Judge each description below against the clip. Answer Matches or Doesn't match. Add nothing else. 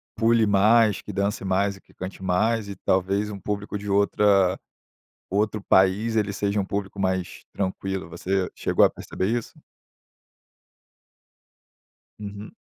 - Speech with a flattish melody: Matches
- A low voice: Matches